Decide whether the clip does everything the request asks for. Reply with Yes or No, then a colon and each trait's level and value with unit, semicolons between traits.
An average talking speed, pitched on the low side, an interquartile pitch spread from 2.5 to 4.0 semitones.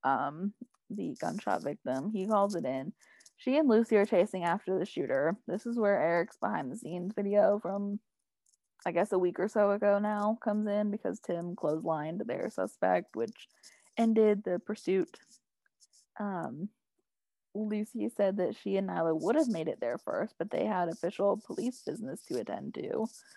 No: average, 165 wpm; high, 205 Hz; average, 3.6 semitones